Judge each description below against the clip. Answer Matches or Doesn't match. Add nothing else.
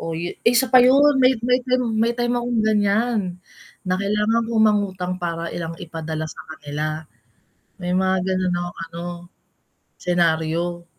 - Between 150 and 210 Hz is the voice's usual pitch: Matches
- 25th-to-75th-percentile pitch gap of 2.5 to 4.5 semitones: Doesn't match